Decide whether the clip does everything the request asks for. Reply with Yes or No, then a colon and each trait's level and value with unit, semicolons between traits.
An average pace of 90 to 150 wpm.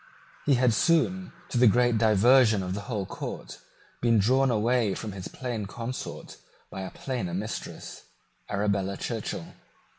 Yes: average, 145 wpm